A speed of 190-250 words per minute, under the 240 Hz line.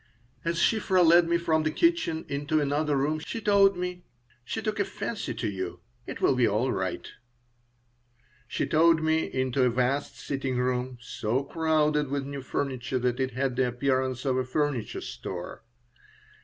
No: average, 165 wpm; medium, 140 Hz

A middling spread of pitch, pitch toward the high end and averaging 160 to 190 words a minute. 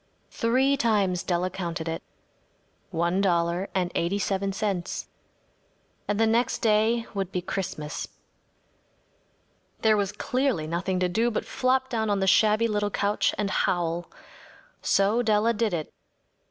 No: average, 3.8 semitones; high, 200 Hz; average, 140 wpm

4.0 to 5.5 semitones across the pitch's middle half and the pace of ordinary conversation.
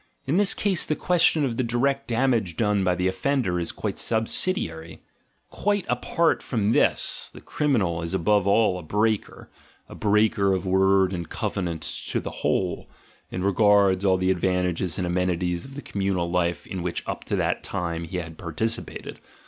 Yes: average, 4.4 semitones; average, 175 wpm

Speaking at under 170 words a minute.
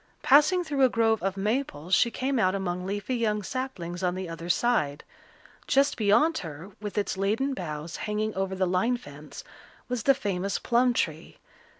No: average, 175 wpm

